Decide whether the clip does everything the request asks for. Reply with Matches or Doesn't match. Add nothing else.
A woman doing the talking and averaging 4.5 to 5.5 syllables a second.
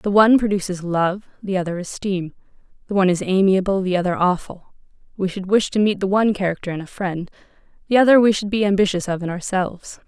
Doesn't match